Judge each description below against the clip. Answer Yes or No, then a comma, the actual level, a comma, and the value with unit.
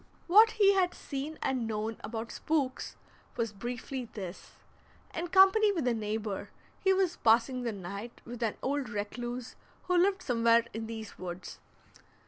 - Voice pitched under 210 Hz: No, high, 240 Hz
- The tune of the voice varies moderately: No, wide, 7.1 semitones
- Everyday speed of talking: Yes, average, 150 wpm